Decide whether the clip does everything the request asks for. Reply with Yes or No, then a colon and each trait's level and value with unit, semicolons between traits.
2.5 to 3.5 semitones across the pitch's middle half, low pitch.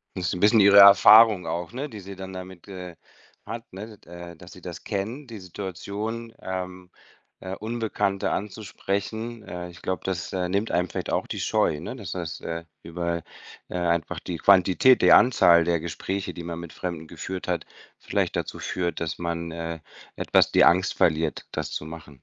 Yes: average, 2.9 semitones; very low, 90 Hz